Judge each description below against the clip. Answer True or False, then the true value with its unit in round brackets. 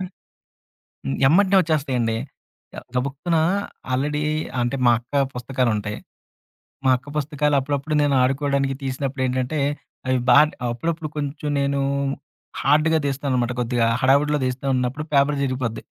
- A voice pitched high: False (140 Hz)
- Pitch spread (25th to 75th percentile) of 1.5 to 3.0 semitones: True (2.6 semitones)